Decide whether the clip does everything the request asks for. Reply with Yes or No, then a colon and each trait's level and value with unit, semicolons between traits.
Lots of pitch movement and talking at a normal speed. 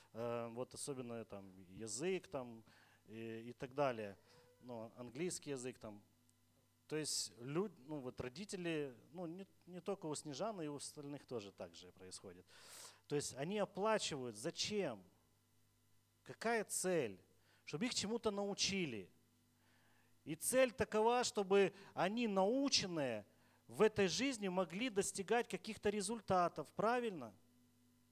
Yes: wide, 9.0 semitones; average, 125 wpm